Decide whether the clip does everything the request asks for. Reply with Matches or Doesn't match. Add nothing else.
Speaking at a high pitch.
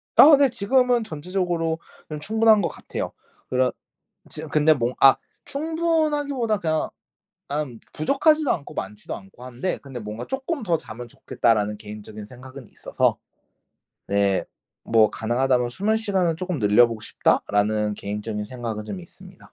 Doesn't match